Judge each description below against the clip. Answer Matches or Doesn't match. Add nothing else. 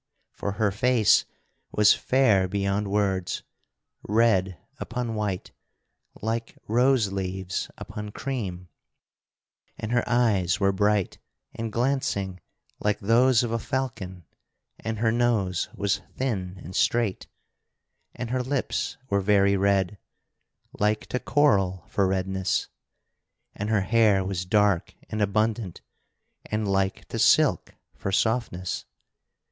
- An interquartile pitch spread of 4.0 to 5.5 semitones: Doesn't match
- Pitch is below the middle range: Matches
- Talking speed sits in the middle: Doesn't match